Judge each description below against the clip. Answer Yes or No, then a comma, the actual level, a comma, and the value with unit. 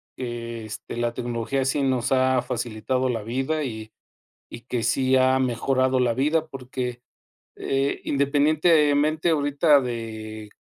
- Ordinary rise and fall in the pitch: Yes, average, 3.1 semitones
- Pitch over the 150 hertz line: No, low, 130 Hz